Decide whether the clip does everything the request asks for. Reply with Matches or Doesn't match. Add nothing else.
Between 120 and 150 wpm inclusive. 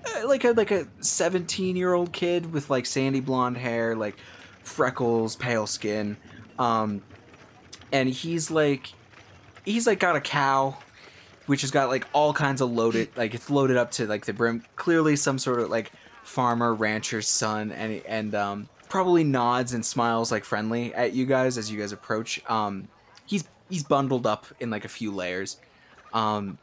Doesn't match